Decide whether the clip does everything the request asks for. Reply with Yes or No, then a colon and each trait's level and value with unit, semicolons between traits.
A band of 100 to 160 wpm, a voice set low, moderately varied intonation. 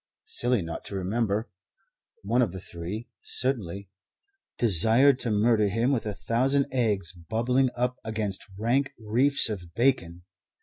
Yes: slow, 135 wpm; low, 110 Hz; average, 4.1 semitones